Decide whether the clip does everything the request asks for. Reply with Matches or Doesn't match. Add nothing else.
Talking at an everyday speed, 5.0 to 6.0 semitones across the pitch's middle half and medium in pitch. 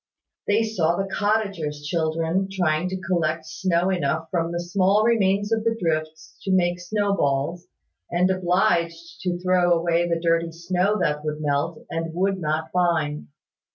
Doesn't match